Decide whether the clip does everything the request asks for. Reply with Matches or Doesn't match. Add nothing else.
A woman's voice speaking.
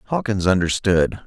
Doesn't match